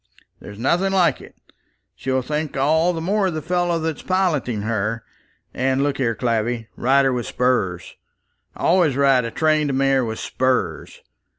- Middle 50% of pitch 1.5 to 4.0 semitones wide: No, average, 4.8 semitones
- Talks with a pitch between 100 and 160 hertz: Yes, low, 135 Hz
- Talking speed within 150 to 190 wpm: Yes, average, 160 wpm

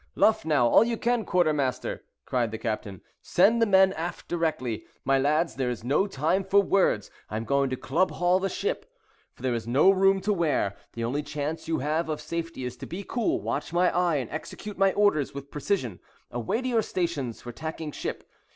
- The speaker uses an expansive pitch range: Yes, wide, 6.7 semitones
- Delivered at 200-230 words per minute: Yes, fast, 205 wpm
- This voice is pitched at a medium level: Yes, medium, 160 Hz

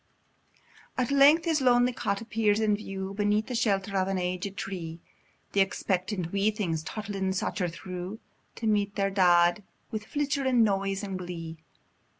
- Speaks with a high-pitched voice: Yes, high, 200 Hz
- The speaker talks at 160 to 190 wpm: No, average, 150 wpm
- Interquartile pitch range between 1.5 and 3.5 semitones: Yes, average, 2.9 semitones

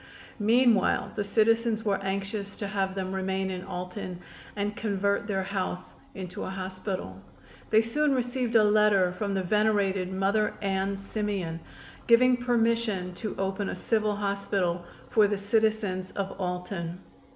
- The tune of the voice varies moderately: No, narrow, 2.3 semitones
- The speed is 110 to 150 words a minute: Yes, average, 140 wpm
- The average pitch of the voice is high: Yes, high, 200 Hz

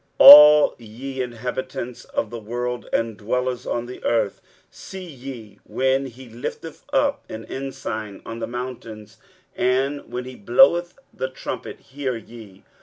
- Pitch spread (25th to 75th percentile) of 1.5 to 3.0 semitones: Yes, average, 2.7 semitones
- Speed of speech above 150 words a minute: No, average, 145 wpm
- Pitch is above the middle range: No, low, 125 Hz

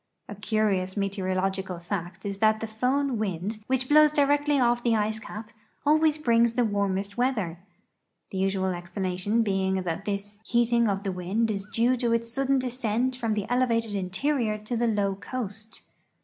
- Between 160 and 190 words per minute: Yes, average, 165 wpm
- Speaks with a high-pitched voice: Yes, high, 215 Hz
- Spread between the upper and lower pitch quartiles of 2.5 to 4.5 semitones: Yes, average, 3.8 semitones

